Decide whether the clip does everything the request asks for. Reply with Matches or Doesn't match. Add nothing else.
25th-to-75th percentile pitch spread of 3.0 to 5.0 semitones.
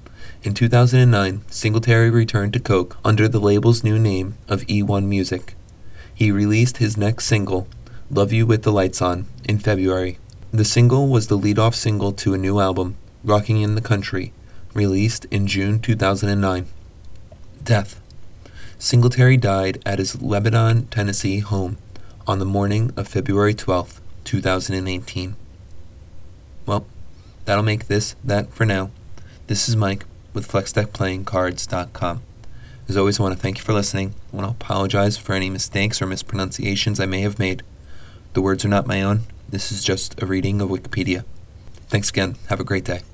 Doesn't match